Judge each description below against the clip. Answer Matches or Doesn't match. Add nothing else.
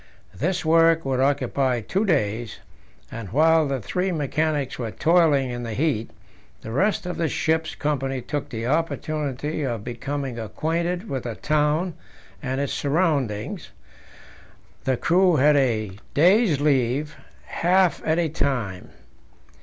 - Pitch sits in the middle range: Matches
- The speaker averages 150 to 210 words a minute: Doesn't match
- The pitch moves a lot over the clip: Doesn't match